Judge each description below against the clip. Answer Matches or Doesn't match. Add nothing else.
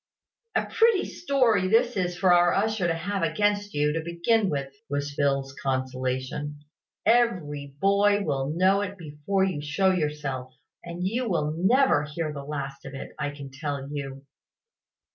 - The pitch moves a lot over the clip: Matches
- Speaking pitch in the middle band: Matches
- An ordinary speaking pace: Matches